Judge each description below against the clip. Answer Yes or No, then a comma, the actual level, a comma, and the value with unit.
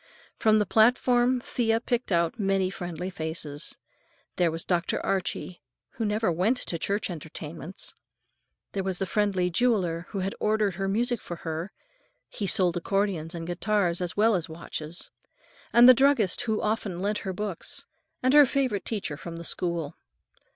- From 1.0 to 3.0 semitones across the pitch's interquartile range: No, average, 4.2 semitones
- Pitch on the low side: No, high, 195 Hz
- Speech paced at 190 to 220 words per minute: No, average, 150 wpm